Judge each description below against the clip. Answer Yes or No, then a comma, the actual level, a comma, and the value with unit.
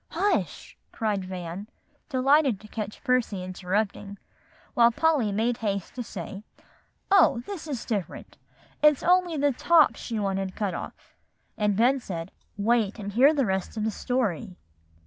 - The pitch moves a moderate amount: Yes, average, 4.9 semitones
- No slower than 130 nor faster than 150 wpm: Yes, average, 145 wpm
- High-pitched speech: Yes, high, 220 Hz